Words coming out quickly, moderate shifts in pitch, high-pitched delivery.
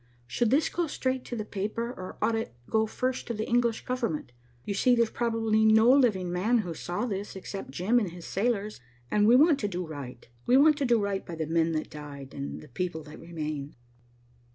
No: fast, 220 wpm; wide, 6.2 semitones; high, 210 Hz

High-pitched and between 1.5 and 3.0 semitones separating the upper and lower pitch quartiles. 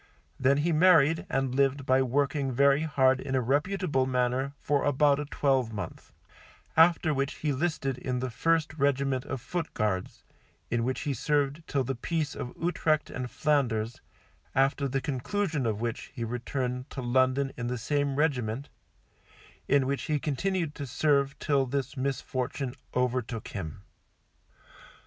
No: low, 135 Hz; narrow, 2.5 semitones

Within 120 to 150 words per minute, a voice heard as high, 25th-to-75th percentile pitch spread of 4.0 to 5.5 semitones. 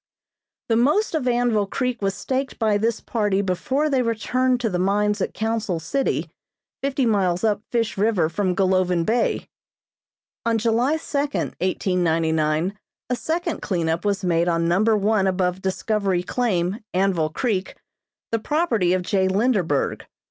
Yes: average, 145 wpm; high, 205 Hz; average, 4.6 semitones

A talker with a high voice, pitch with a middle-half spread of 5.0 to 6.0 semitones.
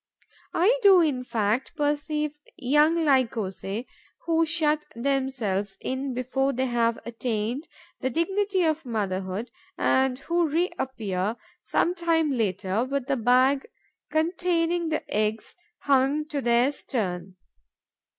Yes: very high, 265 Hz; average, 5.3 semitones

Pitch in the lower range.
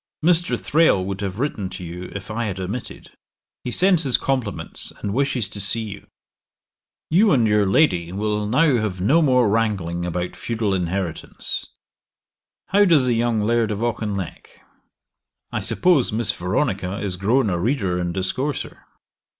Yes: low, 105 Hz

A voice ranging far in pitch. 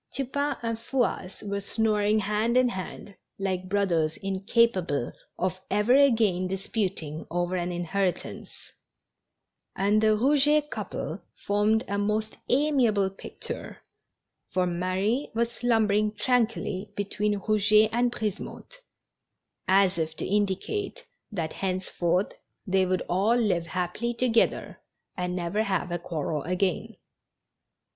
No: average, 3.6 semitones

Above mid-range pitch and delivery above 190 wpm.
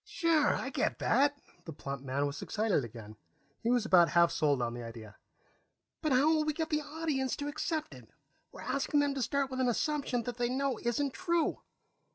Yes: very high, 260 Hz; average, 200 wpm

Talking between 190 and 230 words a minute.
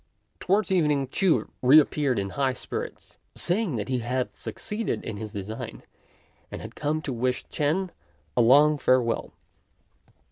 No: average, 145 wpm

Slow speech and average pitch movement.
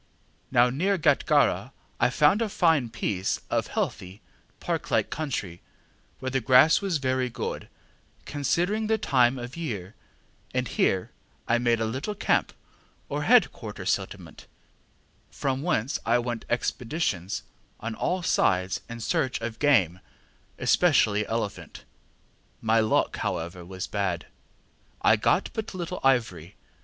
No: slow, 130 wpm; wide, 5.9 semitones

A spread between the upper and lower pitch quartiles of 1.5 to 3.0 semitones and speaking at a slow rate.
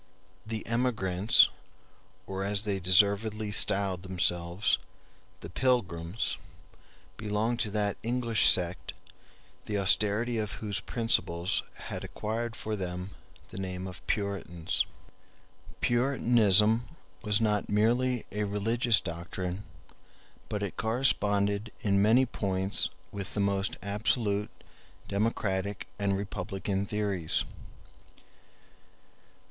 Yes: average, 2.7 semitones; slow, 100 wpm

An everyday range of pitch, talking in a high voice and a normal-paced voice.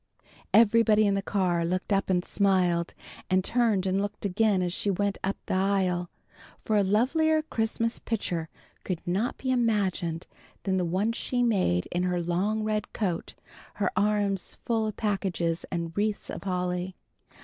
Yes: average, 3.1 semitones; high, 195 Hz; average, 160 wpm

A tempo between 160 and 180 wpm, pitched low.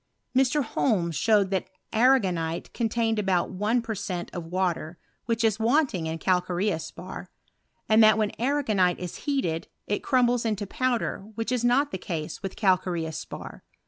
No: average, 165 wpm; high, 205 Hz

